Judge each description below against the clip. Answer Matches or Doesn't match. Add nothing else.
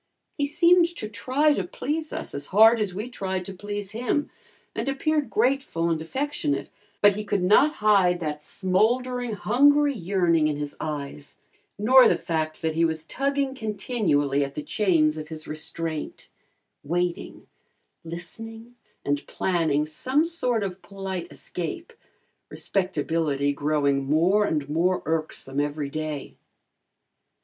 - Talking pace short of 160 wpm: Matches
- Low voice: Doesn't match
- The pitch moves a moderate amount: Doesn't match